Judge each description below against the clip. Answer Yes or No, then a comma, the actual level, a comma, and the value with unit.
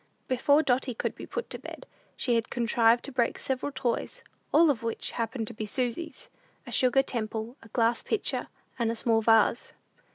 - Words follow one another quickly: No, average, 185 wpm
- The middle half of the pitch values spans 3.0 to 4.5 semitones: No, narrow, 2.6 semitones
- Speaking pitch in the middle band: No, high, 240 Hz